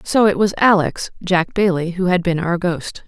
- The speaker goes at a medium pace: No, fast, 215 wpm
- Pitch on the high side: No, medium, 180 Hz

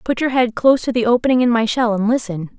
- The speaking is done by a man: No, female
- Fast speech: Yes, fast, 280 wpm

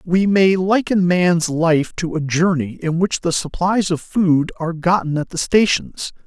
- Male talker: Yes, male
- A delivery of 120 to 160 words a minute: No, average, 180 wpm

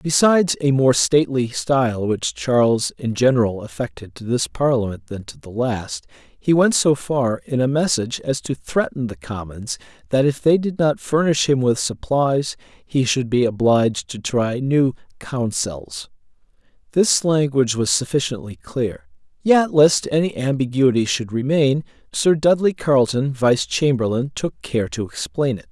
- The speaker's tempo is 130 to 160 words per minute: Yes, average, 155 wpm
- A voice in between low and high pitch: No, low, 130 Hz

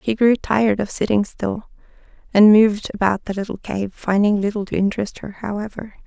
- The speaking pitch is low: No, high, 205 Hz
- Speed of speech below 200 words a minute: Yes, average, 180 wpm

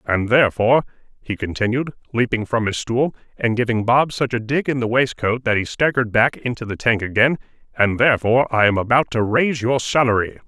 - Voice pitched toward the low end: Yes, low, 120 Hz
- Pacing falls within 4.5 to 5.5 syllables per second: No, 5.8 syllables/s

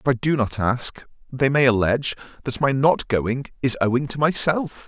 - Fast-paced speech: Yes, fast, 210 wpm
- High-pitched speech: No, low, 130 Hz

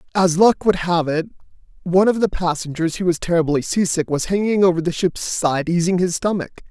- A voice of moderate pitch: Yes, medium, 175 Hz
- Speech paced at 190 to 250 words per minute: Yes, average, 195 wpm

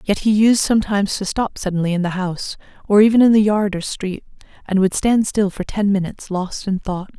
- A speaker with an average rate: No, fast, 225 wpm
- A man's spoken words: No, female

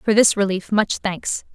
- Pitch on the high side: Yes, high, 200 Hz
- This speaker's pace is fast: No, average, 195 wpm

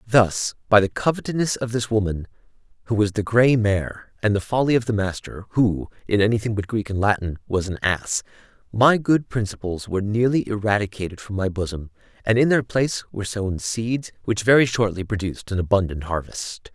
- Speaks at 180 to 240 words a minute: Yes, average, 185 wpm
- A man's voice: Yes, male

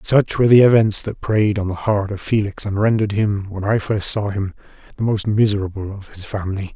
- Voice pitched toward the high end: No, low, 105 Hz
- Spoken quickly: Yes, fast, 220 wpm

